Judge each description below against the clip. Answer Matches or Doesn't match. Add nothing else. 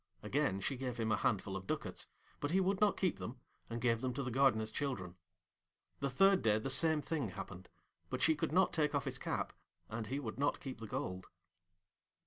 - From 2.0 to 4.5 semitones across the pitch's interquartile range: Doesn't match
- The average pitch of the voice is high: Doesn't match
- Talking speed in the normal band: Doesn't match